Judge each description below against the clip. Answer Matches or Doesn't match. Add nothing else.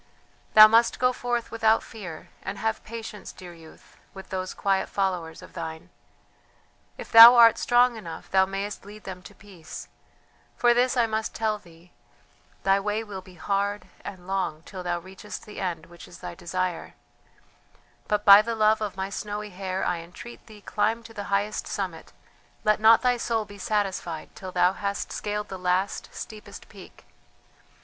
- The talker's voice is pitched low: Doesn't match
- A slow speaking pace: Doesn't match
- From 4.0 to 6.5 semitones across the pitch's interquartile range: Doesn't match